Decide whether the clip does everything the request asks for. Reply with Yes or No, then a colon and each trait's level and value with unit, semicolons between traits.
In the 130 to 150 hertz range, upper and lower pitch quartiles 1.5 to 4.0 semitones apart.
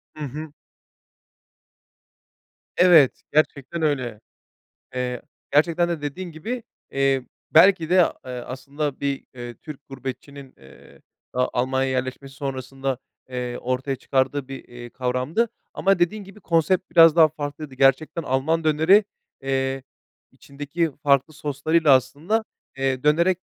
Yes: medium, 140 Hz; average, 3.6 semitones